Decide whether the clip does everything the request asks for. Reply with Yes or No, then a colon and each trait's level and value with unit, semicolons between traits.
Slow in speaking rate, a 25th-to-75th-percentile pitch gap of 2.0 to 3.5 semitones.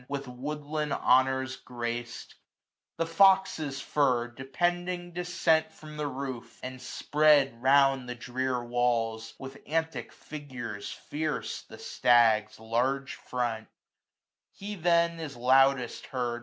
No: slow, 115 wpm; average, 4.0 semitones